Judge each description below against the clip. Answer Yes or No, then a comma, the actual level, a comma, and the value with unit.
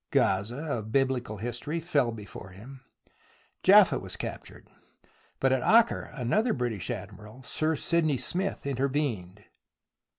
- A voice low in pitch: Yes, low, 130 Hz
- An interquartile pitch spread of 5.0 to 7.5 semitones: Yes, wide, 5.4 semitones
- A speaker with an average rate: No, slow, 120 wpm